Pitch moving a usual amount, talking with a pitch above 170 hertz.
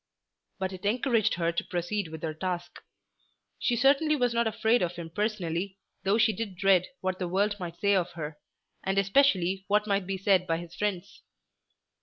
Yes: average, 3.3 semitones; high, 190 Hz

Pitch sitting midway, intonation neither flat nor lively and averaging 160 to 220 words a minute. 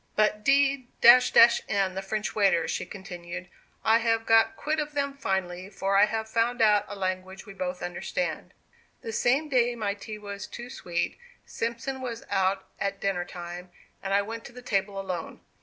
No: high, 205 Hz; average, 3.7 semitones; average, 175 wpm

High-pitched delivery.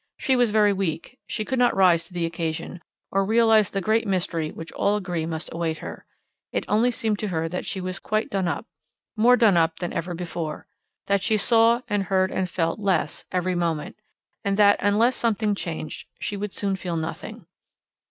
Yes: high, 195 Hz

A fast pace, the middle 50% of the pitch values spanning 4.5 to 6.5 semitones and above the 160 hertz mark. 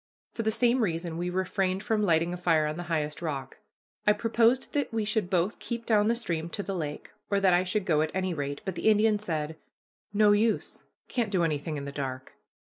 Yes: fast, 220 wpm; average, 4.9 semitones; medium, 185 Hz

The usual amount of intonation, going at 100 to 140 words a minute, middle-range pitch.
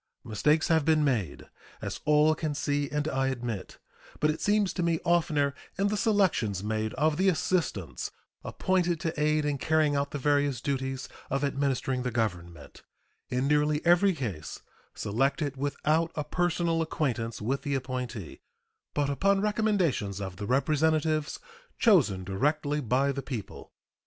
No: average, 4.1 semitones; average, 150 wpm; medium, 145 Hz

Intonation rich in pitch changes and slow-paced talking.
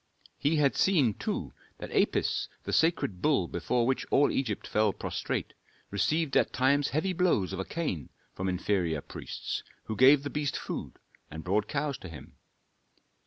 No: wide, 7.5 semitones; average, 165 wpm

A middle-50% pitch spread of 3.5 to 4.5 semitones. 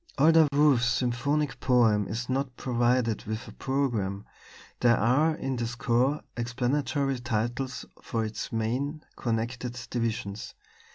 No: average, 2.8 semitones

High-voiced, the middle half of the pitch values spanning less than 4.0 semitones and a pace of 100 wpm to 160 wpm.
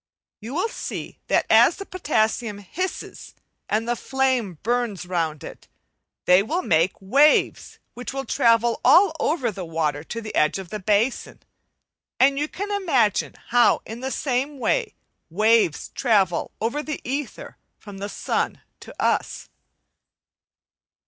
No: high, 230 Hz; wide, 5.6 semitones; average, 140 wpm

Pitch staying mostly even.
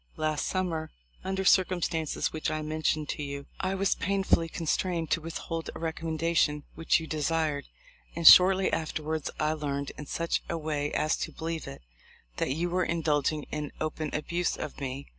Yes: narrow, 1.9 semitones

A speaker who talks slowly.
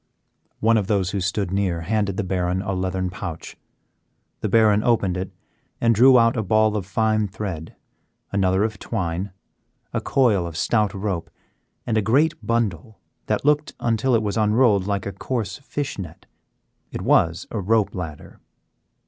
No: average, 165 wpm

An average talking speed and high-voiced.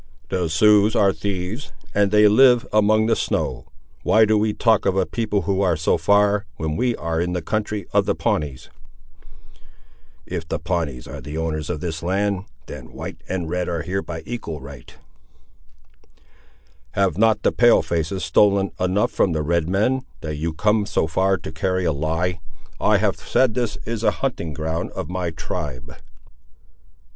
No: average, 175 wpm; very low, 95 Hz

